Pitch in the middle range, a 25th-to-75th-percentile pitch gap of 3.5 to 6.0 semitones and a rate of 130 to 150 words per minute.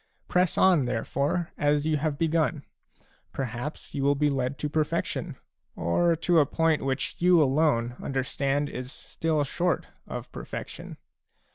No: medium, 145 Hz; average, 3.1 semitones; average, 140 wpm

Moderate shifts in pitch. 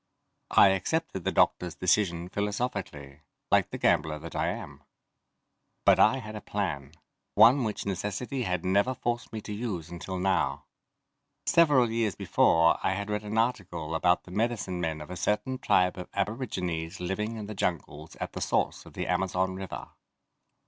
Yes: average, 3.9 semitones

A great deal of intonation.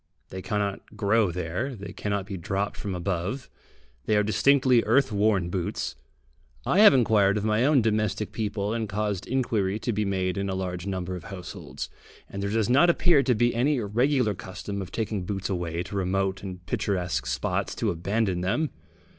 No: average, 3.3 semitones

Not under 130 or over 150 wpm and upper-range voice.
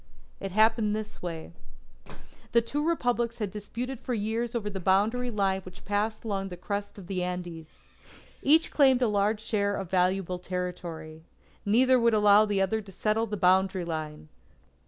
No: average, 165 wpm; high, 205 Hz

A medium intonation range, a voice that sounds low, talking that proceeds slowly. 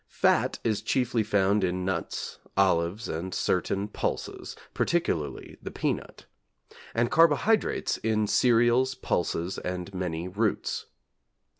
Yes: average, 4.5 semitones; low, 100 Hz; slow, 110 wpm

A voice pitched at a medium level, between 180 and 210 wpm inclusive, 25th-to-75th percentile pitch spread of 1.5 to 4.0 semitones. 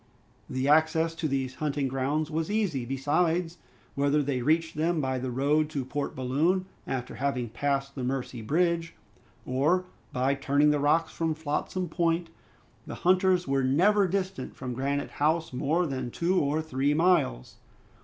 No: medium, 150 Hz; average, 155 wpm; average, 3.7 semitones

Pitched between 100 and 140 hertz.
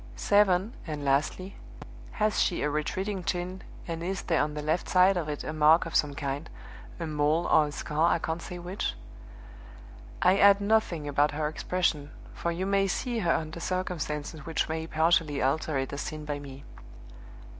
No: medium, 160 Hz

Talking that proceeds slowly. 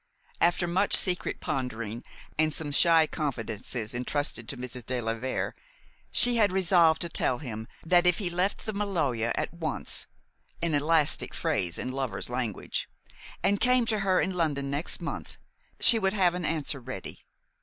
No: average, 165 wpm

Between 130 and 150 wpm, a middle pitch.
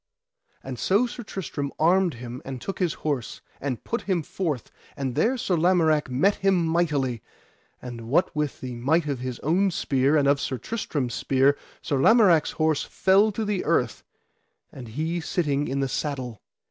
No: average, 170 wpm; medium, 150 Hz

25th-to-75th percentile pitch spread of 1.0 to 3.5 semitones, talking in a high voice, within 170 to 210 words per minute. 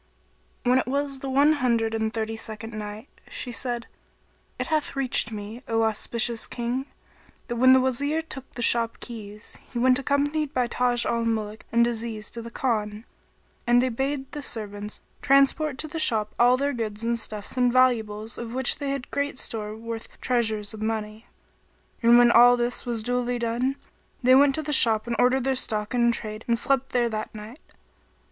Yes: average, 2.8 semitones; high, 240 Hz; average, 185 wpm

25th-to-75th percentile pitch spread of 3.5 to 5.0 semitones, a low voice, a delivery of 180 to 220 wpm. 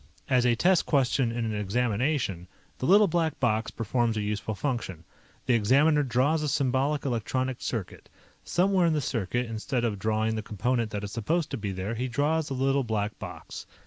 Yes: average, 4.6 semitones; low, 125 Hz; average, 185 wpm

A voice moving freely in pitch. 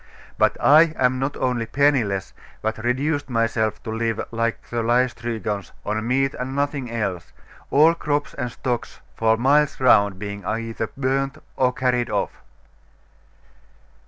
No: average, 3.4 semitones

